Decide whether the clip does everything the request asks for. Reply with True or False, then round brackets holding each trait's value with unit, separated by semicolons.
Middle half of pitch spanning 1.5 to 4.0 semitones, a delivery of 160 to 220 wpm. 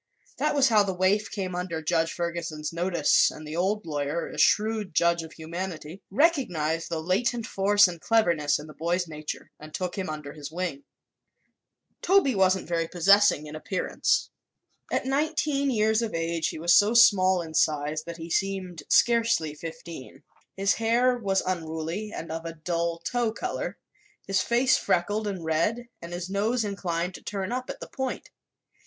False (4.5 semitones; 170 wpm)